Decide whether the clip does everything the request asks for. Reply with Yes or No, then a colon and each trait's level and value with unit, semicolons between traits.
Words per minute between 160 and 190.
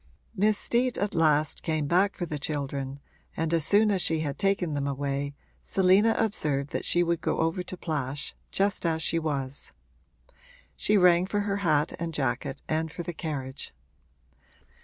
Yes: average, 170 wpm